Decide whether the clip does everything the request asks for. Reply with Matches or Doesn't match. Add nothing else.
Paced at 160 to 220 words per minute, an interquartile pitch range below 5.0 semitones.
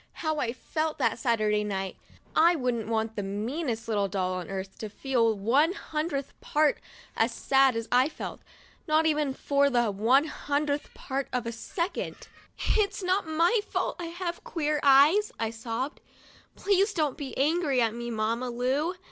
Doesn't match